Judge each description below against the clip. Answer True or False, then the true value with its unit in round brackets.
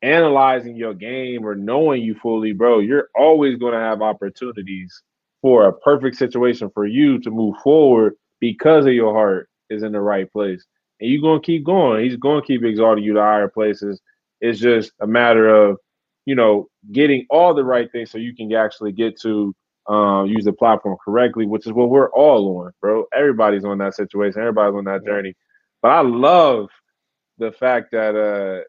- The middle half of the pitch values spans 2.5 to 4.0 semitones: True (3.2 semitones)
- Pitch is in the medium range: False (110 Hz)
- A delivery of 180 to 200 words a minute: True (190 wpm)